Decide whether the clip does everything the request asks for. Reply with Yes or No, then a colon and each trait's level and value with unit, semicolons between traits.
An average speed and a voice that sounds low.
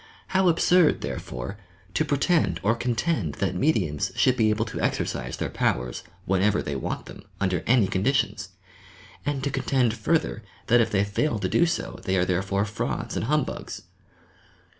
Yes: average, 165 wpm; low, 110 Hz